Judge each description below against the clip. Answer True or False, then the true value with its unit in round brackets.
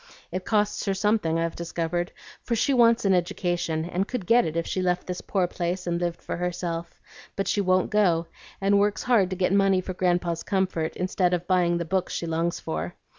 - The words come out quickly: True (210 wpm)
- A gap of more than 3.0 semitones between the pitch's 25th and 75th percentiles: False (2.4 semitones)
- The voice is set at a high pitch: False (180 Hz)